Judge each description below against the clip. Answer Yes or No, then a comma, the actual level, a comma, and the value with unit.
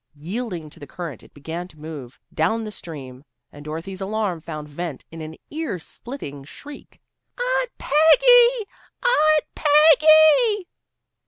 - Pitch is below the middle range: No, high, 190 Hz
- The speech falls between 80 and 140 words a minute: Yes, slow, 135 wpm